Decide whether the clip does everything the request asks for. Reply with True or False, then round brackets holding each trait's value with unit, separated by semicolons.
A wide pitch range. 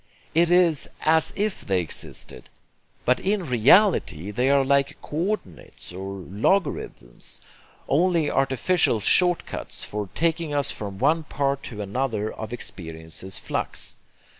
True (8.4 semitones)